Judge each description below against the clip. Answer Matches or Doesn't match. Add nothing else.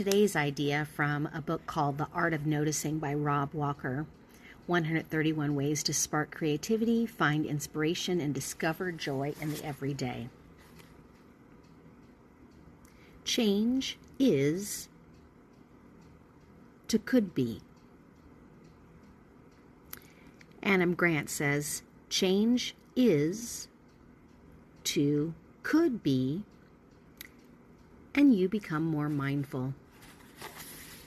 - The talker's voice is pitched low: Doesn't match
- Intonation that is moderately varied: Matches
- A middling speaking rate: Doesn't match